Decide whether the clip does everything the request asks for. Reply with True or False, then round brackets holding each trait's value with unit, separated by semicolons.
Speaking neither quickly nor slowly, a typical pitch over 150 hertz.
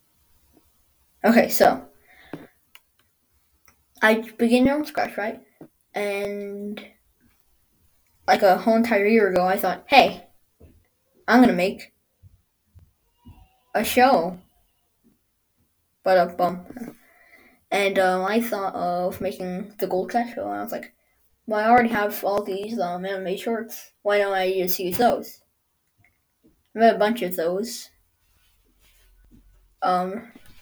False (120 wpm; 185 Hz)